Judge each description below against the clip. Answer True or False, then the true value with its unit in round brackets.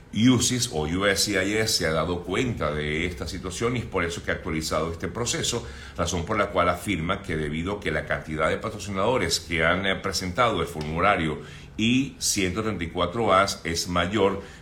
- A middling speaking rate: True (165 wpm)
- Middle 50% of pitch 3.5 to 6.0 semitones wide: True (4.0 semitones)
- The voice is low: True (90 Hz)